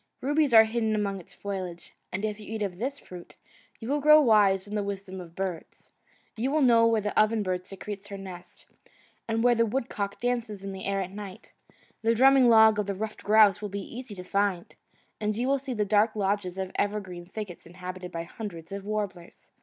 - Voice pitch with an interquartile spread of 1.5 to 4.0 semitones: Yes, average, 2.9 semitones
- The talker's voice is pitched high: Yes, high, 205 Hz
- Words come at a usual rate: No, fast, 215 wpm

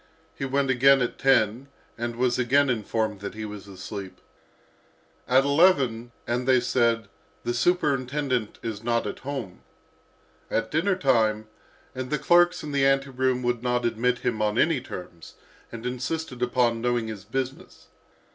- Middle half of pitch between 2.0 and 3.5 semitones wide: Yes, average, 3.1 semitones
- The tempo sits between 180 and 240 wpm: No, average, 155 wpm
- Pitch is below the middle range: Yes, low, 125 Hz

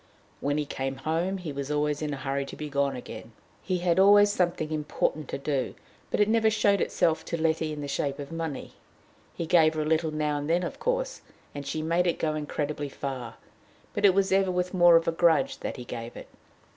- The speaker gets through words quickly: Yes, fast, 225 wpm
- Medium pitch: Yes, medium, 155 Hz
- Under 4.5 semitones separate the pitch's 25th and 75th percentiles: Yes, average, 3.8 semitones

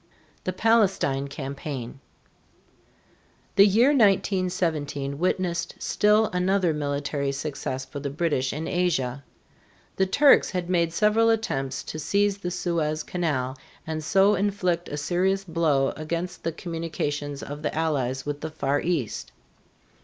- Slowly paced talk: Yes, slow, 130 wpm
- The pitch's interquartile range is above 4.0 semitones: Yes, average, 4.6 semitones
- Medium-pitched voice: Yes, medium, 165 Hz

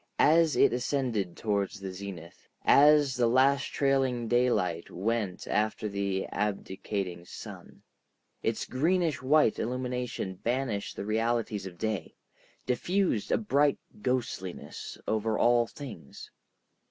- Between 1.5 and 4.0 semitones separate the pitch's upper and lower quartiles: No, average, 4.8 semitones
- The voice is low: Yes, low, 115 Hz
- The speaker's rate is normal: No, slow, 115 wpm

